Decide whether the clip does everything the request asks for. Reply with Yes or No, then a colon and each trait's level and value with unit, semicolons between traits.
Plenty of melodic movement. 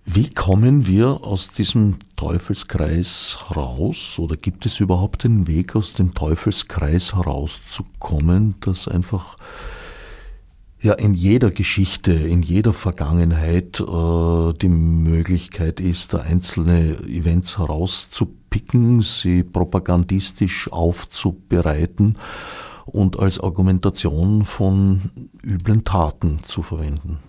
No: average, 2.8 semitones